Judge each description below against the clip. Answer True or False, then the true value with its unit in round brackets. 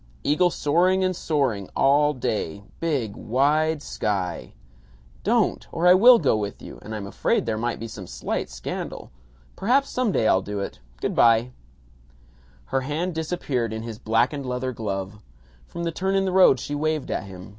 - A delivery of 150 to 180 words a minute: True (175 wpm)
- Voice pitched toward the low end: True (130 Hz)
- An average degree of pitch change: False (7.5 semitones)